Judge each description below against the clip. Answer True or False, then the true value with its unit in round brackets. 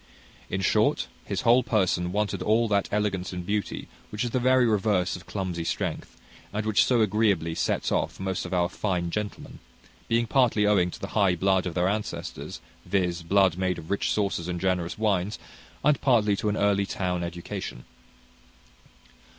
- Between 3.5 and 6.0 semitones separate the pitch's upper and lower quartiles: False (3.0 semitones)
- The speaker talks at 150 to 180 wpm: True (175 wpm)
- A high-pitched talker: False (100 Hz)